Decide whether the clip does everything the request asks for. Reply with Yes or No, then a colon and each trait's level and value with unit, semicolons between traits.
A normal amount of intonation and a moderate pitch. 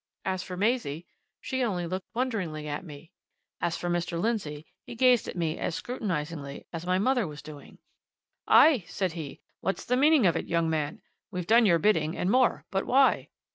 No: wide, 6.0 semitones; medium, 180 Hz